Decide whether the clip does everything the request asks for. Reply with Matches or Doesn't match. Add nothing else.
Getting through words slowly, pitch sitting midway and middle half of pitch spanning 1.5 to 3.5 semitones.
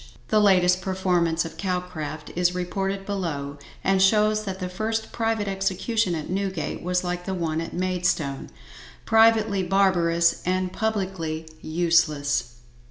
Matches